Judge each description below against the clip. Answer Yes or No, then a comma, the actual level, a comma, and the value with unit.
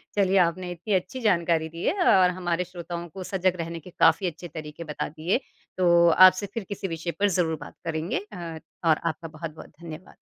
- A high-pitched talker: No, medium, 170 Hz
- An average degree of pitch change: No, narrow, 2.3 semitones